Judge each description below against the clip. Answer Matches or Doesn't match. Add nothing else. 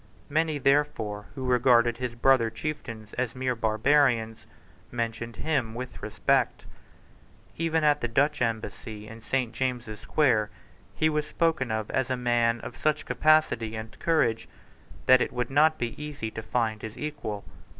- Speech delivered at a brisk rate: Doesn't match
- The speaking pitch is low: Matches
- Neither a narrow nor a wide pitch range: Matches